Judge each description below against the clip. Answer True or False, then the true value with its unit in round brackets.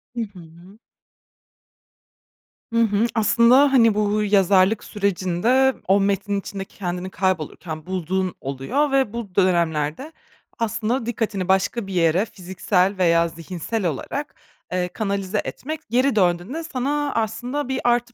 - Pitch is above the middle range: True (200 Hz)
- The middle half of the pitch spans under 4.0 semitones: False (4.5 semitones)